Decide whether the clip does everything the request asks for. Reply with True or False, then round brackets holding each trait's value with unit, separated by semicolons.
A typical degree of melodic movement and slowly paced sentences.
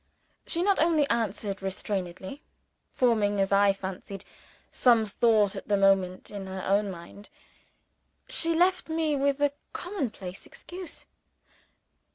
False (6.9 semitones; 125 wpm)